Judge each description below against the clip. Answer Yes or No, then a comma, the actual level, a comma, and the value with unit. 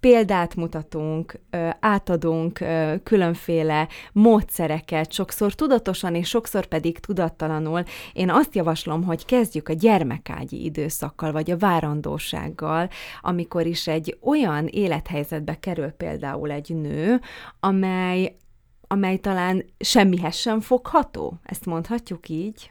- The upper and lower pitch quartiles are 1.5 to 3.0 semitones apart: No, average, 3.8 semitones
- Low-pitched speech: No, medium, 170 Hz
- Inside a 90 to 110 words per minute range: Yes, slow, 105 wpm